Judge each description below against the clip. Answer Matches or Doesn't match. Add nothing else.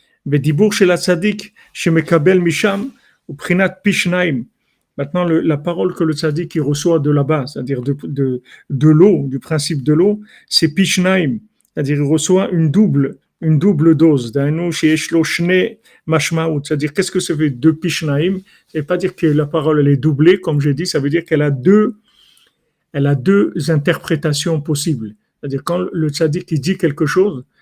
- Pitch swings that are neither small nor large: Matches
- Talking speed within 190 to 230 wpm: Doesn't match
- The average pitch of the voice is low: Doesn't match